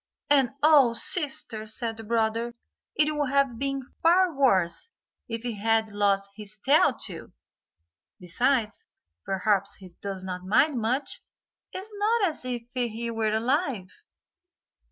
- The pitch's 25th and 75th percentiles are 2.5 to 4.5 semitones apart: No, average, 4.9 semitones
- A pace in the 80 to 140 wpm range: Yes, slow, 135 wpm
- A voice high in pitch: Yes, high, 230 Hz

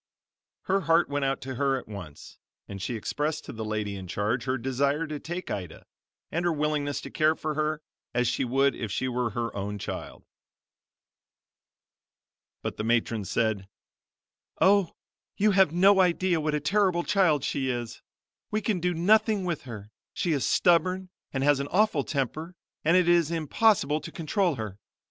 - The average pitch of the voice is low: No, medium, 150 Hz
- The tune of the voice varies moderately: No, wide, 6.3 semitones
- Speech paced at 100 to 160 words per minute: No, average, 175 wpm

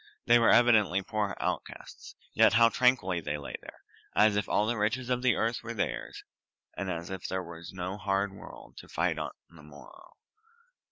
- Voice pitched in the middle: No, low, 100 Hz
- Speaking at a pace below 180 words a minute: No, average, 185 wpm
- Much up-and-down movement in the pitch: No, average, 4.3 semitones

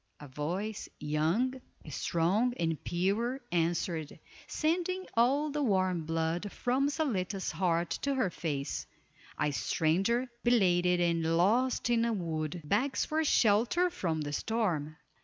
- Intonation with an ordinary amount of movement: No, wide, 7.0 semitones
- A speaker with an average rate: No, slow, 125 wpm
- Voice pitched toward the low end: No, medium, 185 Hz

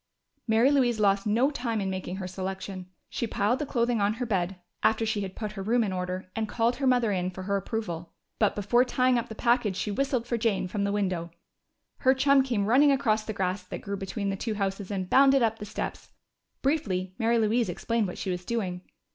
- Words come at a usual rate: No, fast, 220 wpm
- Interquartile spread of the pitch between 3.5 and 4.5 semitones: Yes, average, 3.8 semitones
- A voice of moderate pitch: No, high, 215 Hz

